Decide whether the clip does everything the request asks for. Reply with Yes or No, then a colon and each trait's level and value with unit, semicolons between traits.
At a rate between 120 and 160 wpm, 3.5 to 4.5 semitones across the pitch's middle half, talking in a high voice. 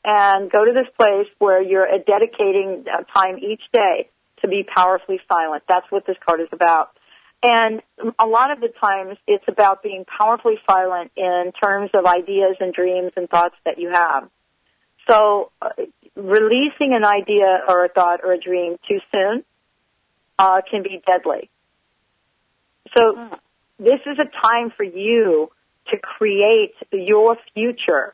Yes: average, 150 wpm; average, 4.1 semitones; high, 205 Hz